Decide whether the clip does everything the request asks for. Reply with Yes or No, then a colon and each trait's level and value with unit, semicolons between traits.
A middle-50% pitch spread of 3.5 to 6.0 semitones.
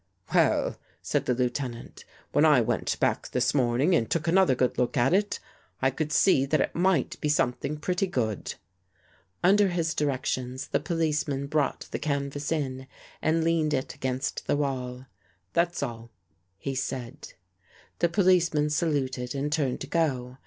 Yes: average, 4.2 semitones